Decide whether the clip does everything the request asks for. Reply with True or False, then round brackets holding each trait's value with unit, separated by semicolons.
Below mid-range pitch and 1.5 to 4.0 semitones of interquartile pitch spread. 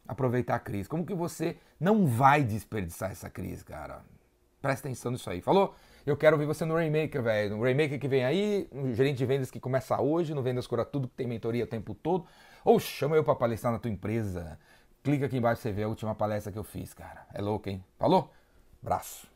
False (125 Hz; 5.5 semitones)